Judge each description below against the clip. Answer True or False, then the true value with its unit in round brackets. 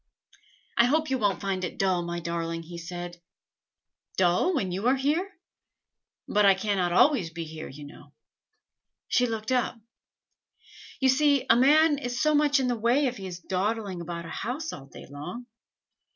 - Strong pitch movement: True (7.2 semitones)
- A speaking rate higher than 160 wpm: True (175 wpm)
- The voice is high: True (205 Hz)